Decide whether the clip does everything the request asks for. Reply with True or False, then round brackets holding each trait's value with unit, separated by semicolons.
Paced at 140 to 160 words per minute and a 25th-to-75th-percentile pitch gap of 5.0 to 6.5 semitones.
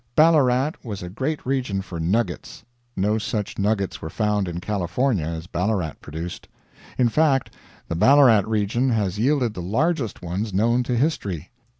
True (155 wpm; 5.6 semitones)